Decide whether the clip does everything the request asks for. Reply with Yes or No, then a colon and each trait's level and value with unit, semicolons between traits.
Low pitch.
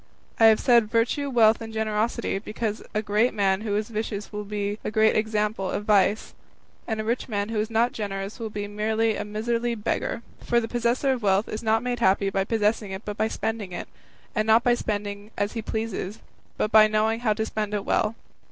No: high, 215 Hz